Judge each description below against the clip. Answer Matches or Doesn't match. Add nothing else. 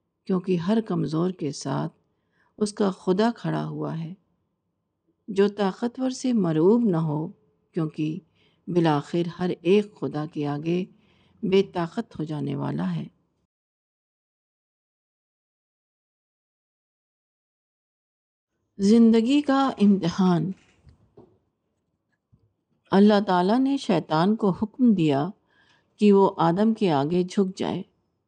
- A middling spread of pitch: Matches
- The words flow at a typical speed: Doesn't match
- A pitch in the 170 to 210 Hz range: Matches